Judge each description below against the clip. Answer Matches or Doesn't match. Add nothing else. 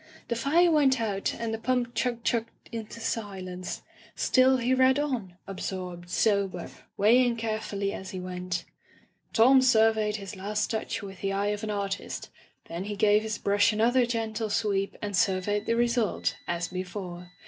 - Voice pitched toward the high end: Matches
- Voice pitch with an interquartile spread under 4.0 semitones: Matches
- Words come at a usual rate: Matches